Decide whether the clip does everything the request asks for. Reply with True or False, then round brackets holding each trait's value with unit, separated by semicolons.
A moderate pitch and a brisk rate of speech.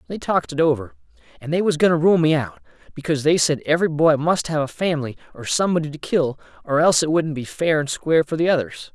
True (155 Hz; 240 wpm)